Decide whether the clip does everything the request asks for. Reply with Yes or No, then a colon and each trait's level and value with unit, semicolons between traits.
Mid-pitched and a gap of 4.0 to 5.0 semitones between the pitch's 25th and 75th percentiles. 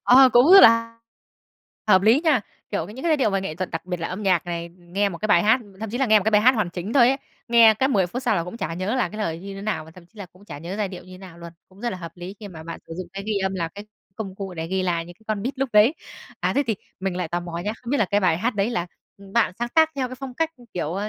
No: high, 200 Hz; average, 4.6 semitones